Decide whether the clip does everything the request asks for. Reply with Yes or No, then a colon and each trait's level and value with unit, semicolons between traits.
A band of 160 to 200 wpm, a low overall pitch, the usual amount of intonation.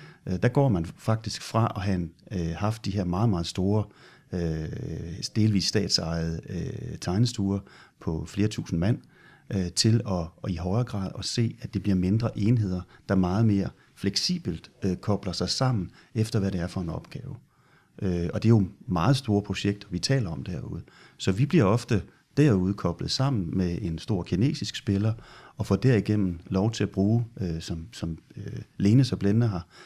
Yes: average, 165 wpm; low, 100 Hz; average, 3.8 semitones